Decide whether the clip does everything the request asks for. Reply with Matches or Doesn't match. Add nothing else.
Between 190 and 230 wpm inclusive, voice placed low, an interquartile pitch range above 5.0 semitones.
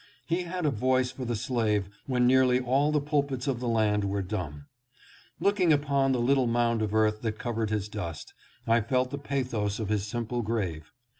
Doesn't match